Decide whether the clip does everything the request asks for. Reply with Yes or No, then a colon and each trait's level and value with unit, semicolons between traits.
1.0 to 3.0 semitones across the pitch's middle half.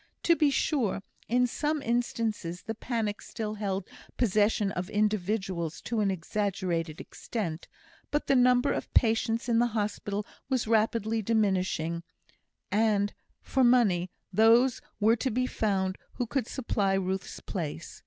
No: average, 3.6 semitones